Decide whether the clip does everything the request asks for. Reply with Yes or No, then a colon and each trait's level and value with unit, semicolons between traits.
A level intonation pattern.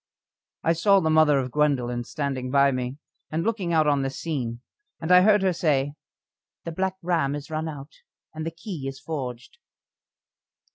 No: average, 3.6 semitones